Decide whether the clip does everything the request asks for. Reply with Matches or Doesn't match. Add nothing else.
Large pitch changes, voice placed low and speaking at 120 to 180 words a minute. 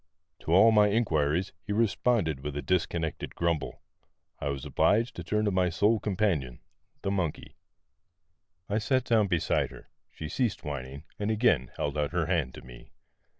Matches